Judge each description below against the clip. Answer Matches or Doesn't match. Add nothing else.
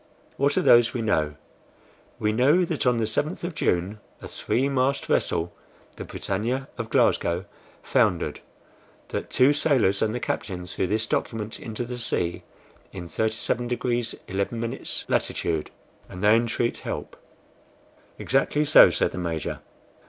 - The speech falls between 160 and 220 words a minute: Doesn't match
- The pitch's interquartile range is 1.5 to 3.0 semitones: Doesn't match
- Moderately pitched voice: Doesn't match